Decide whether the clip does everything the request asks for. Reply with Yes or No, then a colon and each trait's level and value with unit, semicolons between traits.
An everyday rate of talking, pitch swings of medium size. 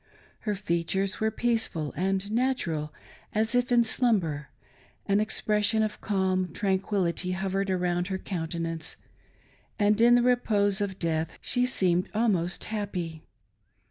No: slow, 125 wpm; average, 3.7 semitones